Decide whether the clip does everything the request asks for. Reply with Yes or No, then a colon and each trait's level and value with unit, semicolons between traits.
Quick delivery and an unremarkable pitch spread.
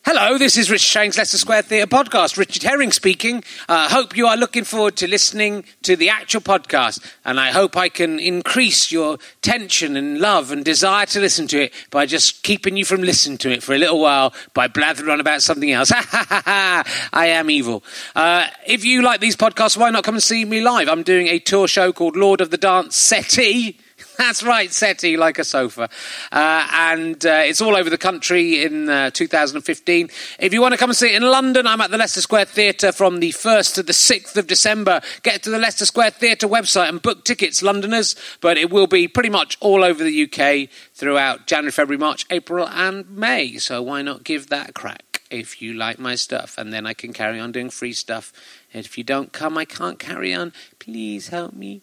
No: fast, 220 wpm; wide, 6.1 semitones